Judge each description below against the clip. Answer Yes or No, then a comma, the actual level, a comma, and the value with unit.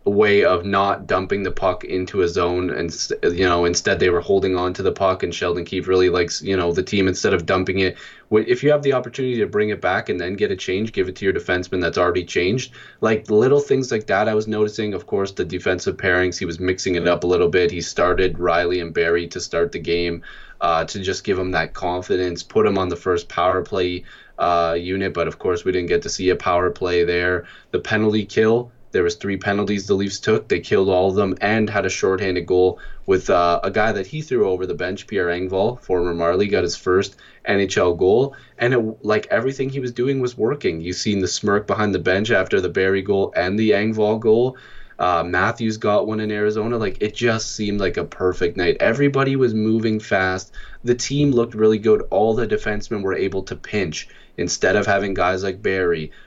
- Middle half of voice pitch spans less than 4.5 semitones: Yes, average, 3.4 semitones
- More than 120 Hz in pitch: No, low, 100 Hz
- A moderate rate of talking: No, fast, 225 wpm